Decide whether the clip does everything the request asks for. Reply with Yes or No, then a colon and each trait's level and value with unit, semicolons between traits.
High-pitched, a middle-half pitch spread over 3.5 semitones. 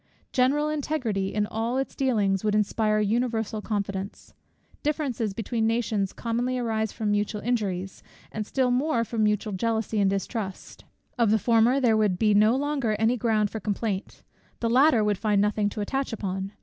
No: high, 220 Hz; average, 2.7 semitones